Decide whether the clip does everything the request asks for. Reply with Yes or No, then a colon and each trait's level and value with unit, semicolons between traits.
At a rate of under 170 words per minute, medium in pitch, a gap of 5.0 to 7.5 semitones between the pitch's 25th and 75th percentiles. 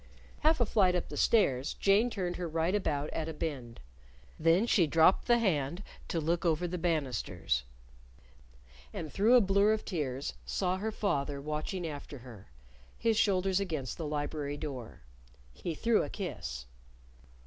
Yes: average, 160 wpm; medium, 165 Hz; average, 5.3 semitones